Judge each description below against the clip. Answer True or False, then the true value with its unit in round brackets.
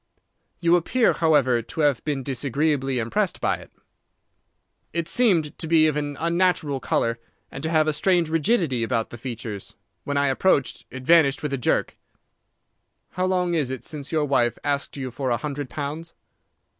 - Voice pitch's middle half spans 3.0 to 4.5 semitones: True (3.8 semitones)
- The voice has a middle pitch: True (145 Hz)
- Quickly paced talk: False (170 wpm)